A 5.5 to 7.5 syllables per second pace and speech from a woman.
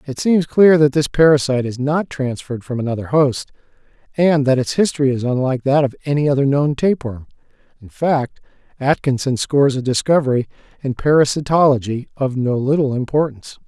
No: 5.8 syllables/s; male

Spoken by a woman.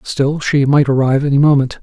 No: male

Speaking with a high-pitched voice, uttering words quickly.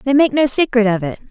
Yes: high, 245 Hz; fast, 275 wpm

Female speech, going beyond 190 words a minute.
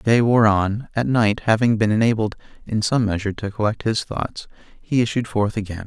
No: male; fast, 205 wpm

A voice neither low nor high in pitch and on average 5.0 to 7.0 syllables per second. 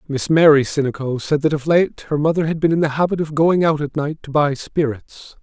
Yes: medium, 150 Hz; 5.4 syllables/s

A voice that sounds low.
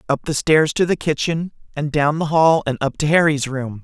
No: medium, 150 Hz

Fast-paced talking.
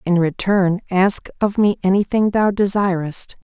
No: slow, 135 wpm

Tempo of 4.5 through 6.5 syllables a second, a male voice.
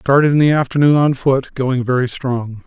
Yes: 5.0 syllables/s; male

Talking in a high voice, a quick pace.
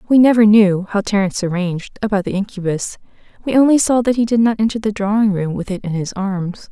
Yes: high, 205 Hz; fast, 225 wpm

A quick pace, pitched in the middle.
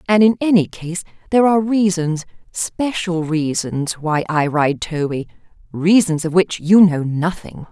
No: average, 140 wpm; medium, 175 Hz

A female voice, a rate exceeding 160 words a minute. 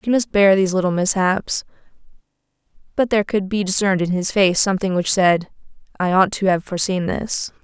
Yes: female; average, 180 wpm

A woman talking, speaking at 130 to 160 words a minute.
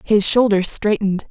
Yes: female; average, 140 wpm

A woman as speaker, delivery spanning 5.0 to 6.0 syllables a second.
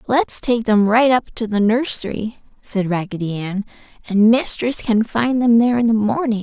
No: female; 4.8 syllables/s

